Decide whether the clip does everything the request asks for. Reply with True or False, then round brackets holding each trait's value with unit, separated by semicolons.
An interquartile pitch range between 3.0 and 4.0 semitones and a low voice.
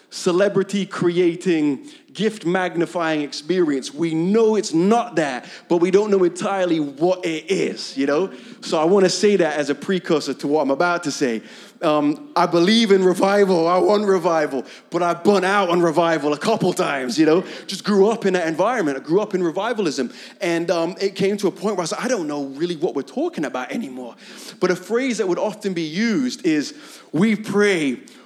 False (3.6 semitones; 180 Hz)